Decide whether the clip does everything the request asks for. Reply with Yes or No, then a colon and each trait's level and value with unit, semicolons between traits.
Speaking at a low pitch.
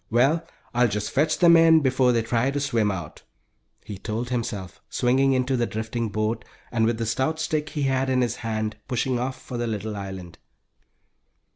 Yes: low, 120 Hz